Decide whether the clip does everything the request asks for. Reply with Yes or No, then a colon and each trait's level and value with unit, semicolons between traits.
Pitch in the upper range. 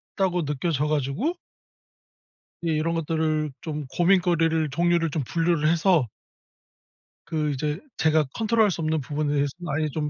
No: medium, 160 Hz